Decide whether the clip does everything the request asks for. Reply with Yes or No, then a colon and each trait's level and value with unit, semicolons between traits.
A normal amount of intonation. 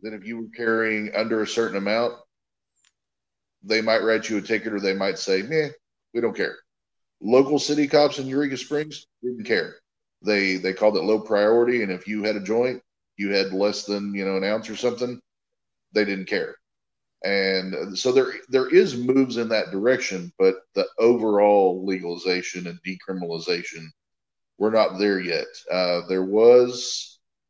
Yes: average, 4.3 semitones